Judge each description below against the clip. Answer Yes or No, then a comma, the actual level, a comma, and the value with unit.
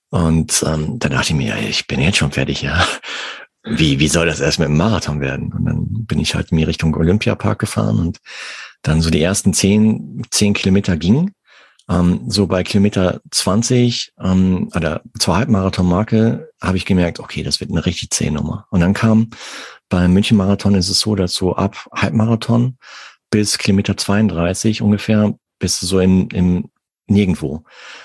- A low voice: Yes, low, 100 Hz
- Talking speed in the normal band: Yes, average, 165 wpm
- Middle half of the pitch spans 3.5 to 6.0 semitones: Yes, average, 3.9 semitones